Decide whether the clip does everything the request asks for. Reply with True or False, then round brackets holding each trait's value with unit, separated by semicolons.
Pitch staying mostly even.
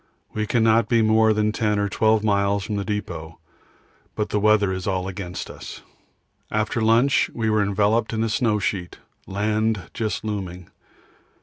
True (1.7 semitones)